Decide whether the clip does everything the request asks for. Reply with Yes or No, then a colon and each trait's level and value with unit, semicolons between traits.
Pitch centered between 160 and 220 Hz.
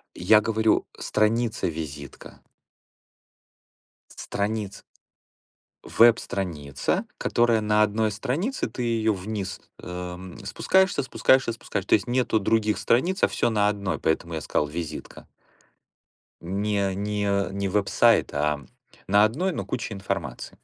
No: low, 105 Hz